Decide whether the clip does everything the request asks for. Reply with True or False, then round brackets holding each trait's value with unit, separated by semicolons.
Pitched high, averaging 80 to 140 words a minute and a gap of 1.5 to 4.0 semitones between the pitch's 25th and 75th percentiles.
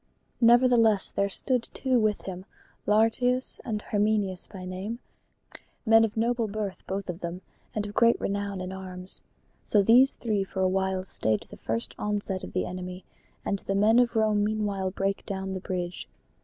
False (200 Hz; 170 wpm; 2.9 semitones)